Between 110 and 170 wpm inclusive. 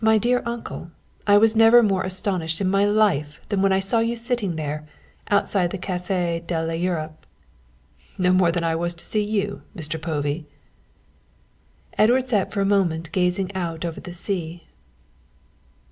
Yes: average, 160 wpm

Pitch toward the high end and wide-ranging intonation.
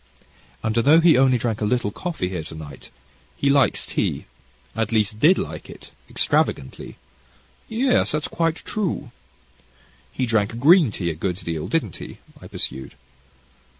No: low, 115 Hz; wide, 7.8 semitones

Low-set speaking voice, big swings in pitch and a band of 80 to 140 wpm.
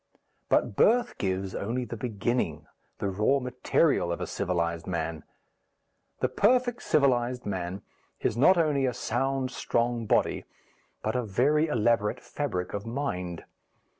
Yes: low, 120 Hz; wide, 5.8 semitones; slow, 135 wpm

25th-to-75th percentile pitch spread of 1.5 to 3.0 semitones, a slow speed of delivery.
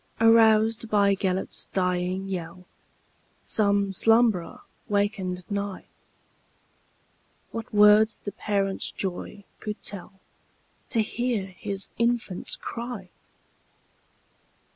Yes: narrow, 2.6 semitones; slow, 75 wpm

